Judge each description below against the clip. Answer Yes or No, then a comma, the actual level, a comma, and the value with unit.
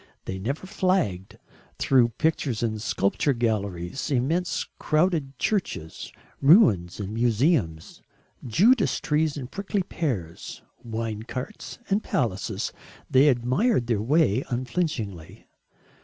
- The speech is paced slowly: Yes, slow, 105 wpm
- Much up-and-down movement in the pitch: Yes, wide, 7.0 semitones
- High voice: No, low, 125 Hz